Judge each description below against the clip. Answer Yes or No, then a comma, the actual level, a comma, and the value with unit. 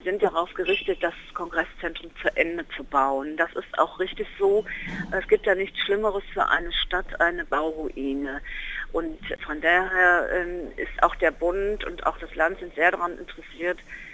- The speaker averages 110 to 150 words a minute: No, average, 165 wpm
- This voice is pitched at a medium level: Yes, medium, 180 Hz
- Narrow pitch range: No, average, 4.1 semitones